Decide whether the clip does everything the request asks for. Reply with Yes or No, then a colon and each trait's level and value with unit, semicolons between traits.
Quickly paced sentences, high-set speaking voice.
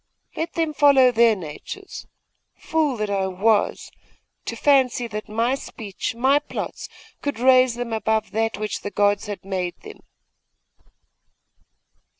No: slow, 135 wpm; high, 230 Hz